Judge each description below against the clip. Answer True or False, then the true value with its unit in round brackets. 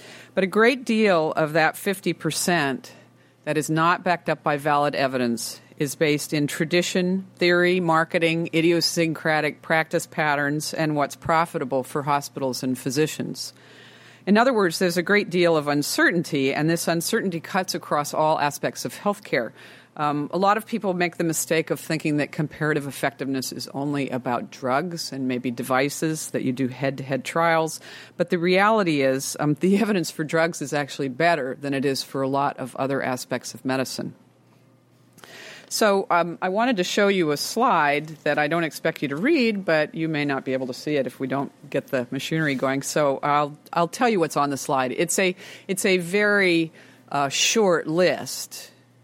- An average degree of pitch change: True (4.1 semitones)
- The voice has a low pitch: False (155 Hz)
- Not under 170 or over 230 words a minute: True (185 wpm)